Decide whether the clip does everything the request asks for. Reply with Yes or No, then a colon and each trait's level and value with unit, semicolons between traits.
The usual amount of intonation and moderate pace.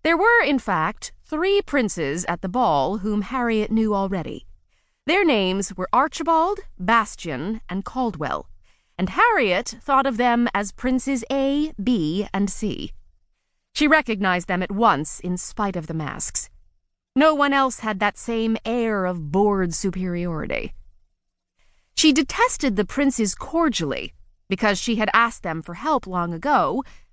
No: wide, 6.9 semitones; average, 145 wpm